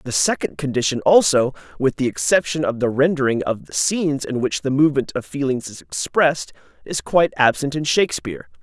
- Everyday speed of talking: Yes, average, 180 wpm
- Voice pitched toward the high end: No, low, 135 Hz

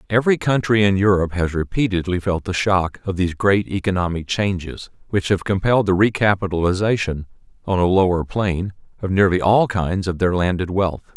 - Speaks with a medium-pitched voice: No, very low, 95 Hz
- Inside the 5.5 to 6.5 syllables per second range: Yes, 5.6 syllables/s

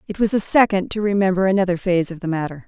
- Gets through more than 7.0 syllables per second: Yes, 7.2 syllables/s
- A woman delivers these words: Yes, female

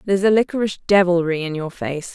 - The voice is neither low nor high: Yes, medium, 180 Hz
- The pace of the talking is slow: No, average, 195 wpm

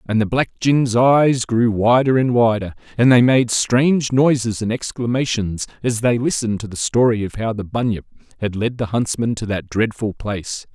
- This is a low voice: Yes, low, 115 Hz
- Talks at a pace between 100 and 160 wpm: No, average, 190 wpm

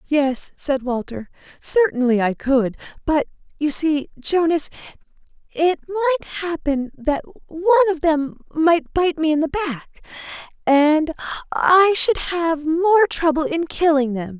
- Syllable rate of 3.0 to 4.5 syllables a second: Yes, 4.0 syllables/s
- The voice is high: Yes, very high, 310 Hz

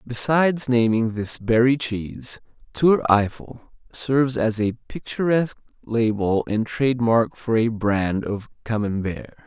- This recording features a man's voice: Yes, male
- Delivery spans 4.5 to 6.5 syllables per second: No, 4.1 syllables/s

